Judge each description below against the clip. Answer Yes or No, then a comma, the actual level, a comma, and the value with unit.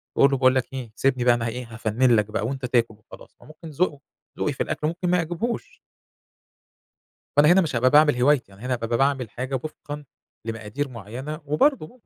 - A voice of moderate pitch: No, low, 130 Hz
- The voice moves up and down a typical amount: Yes, average, 4.3 semitones